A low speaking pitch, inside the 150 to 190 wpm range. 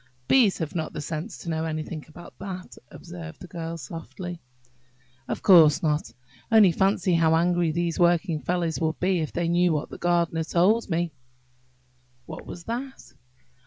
No: medium, 170 Hz; average, 165 wpm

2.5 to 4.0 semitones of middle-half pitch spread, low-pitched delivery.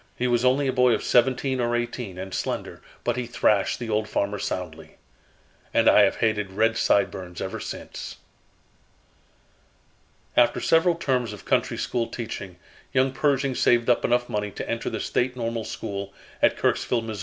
Yes: average, 3.4 semitones; low, 120 Hz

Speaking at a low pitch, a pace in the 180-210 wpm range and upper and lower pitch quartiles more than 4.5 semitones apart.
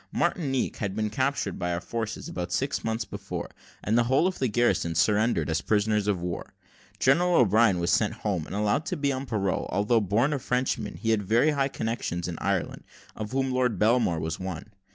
Yes: low, 110 Hz; average, 200 wpm; average, 4.9 semitones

